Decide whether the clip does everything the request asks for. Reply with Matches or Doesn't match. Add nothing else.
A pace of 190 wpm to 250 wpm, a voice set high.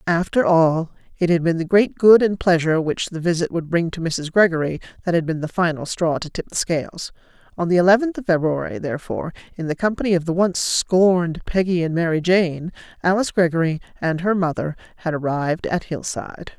Doesn't match